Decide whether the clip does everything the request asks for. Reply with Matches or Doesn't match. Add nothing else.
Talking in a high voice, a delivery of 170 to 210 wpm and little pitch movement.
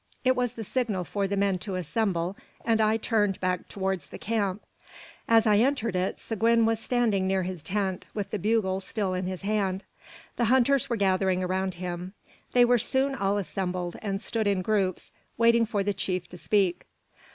Doesn't match